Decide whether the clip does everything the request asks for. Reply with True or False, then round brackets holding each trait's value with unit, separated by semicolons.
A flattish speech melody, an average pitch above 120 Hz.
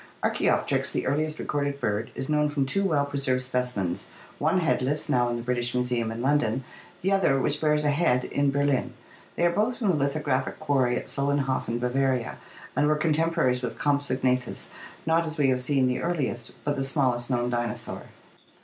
False (3.1 semitones; 135 Hz)